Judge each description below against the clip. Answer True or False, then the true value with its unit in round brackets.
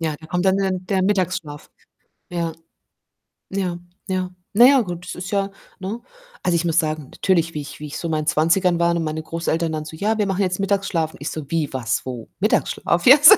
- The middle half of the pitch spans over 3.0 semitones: True (3.4 semitones)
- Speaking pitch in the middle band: True (175 Hz)